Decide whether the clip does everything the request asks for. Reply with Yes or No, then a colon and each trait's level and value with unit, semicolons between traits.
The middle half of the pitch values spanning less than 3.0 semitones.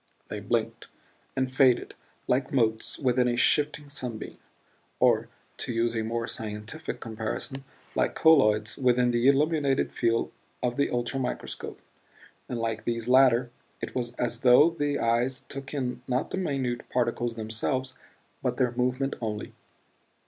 Yes: narrow, 2.5 semitones